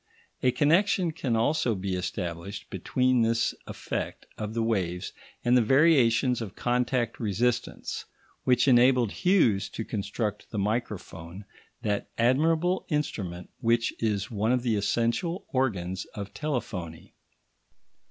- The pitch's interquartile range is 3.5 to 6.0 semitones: Yes, average, 4.2 semitones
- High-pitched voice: No, low, 115 Hz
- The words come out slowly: Yes, slow, 125 wpm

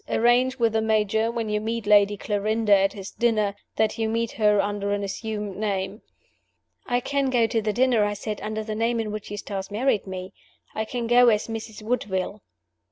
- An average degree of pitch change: No, narrow, 1.9 semitones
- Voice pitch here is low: No, high, 215 Hz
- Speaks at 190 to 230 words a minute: Yes, average, 195 wpm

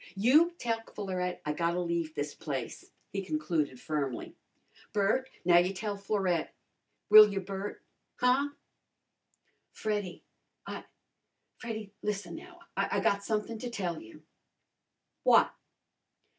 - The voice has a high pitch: Yes, high, 195 Hz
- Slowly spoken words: Yes, slow, 115 wpm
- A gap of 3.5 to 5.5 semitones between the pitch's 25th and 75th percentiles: Yes, average, 4.1 semitones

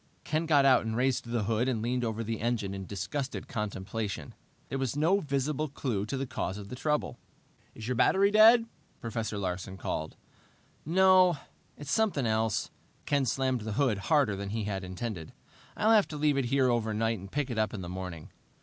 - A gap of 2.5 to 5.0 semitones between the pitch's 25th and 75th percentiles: No, wide, 5.4 semitones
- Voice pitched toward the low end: Yes, low, 120 Hz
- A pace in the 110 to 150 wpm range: No, average, 195 wpm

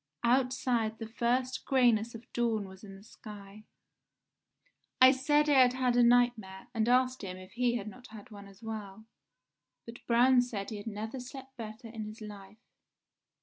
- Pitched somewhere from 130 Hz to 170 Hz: No, high, 230 Hz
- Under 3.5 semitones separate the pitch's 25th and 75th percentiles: Yes, average, 2.9 semitones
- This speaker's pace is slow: No, average, 175 wpm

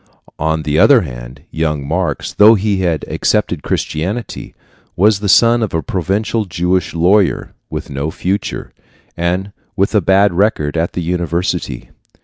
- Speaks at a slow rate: No, average, 145 wpm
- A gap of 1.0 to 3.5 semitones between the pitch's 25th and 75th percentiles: No, average, 4.1 semitones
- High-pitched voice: No, very low, 90 Hz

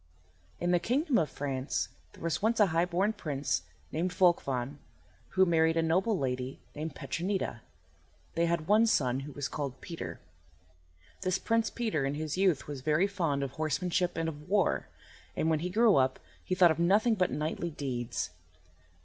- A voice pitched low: No, medium, 165 Hz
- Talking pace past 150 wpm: Yes, average, 175 wpm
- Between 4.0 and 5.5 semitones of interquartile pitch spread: Yes, average, 4.6 semitones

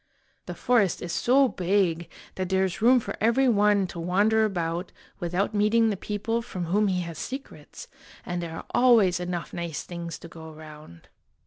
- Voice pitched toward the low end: No, medium, 185 Hz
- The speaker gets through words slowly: No, average, 180 wpm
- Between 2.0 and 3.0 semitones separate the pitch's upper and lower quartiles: No, average, 4.2 semitones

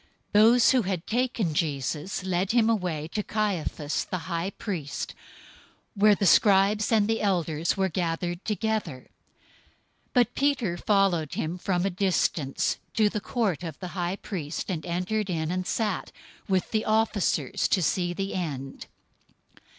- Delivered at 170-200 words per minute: No, average, 150 wpm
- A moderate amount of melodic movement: Yes, average, 4.0 semitones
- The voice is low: No, medium, 185 Hz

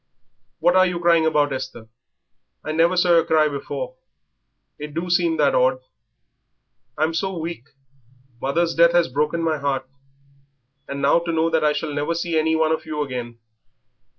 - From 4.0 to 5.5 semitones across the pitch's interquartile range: No, average, 2.7 semitones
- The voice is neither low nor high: Yes, medium, 160 Hz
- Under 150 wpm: No, average, 170 wpm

